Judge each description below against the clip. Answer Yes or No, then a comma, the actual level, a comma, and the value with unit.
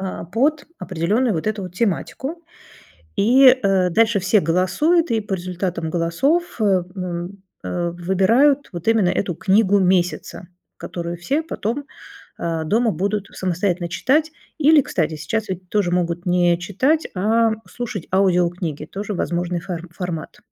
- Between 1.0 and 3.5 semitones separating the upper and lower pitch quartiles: No, average, 4.5 semitones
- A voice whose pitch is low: No, high, 190 Hz